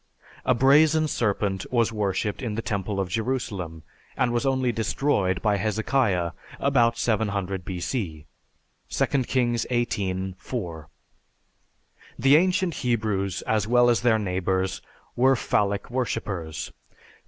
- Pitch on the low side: Yes, low, 110 Hz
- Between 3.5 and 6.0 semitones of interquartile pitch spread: Yes, average, 4.3 semitones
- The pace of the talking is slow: Yes, slow, 120 wpm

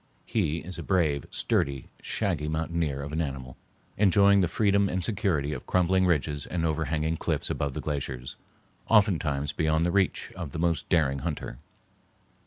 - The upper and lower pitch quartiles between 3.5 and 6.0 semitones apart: Yes, average, 4.2 semitones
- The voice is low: Yes, very low, 80 Hz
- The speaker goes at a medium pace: Yes, average, 160 wpm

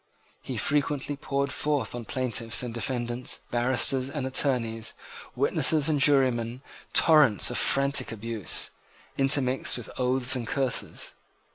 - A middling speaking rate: No, slow, 120 wpm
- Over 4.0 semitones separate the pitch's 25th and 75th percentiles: No, narrow, 2.6 semitones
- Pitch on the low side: Yes, low, 130 Hz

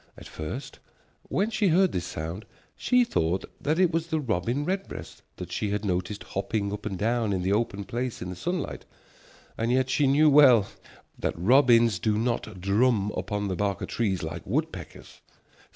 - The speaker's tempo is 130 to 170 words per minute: No, average, 180 wpm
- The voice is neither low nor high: No, low, 115 Hz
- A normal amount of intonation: No, wide, 6.4 semitones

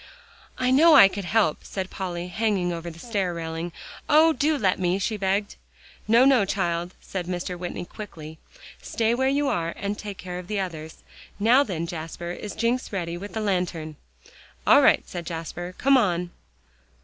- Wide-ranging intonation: No, average, 4.2 semitones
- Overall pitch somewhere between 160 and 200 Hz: Yes, medium, 185 Hz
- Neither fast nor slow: Yes, average, 175 wpm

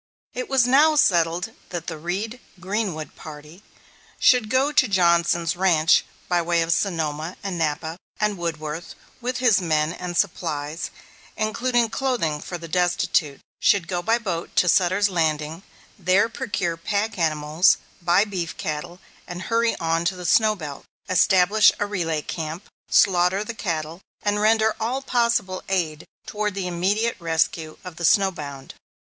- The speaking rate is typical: Yes, average, 150 wpm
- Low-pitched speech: No, medium, 180 Hz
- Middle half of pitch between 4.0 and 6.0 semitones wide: Yes, average, 4.4 semitones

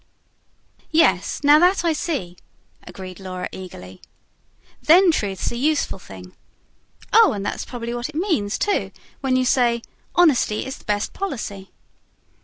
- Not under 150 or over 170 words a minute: No, average, 140 wpm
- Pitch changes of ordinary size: No, wide, 8.4 semitones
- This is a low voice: No, high, 240 Hz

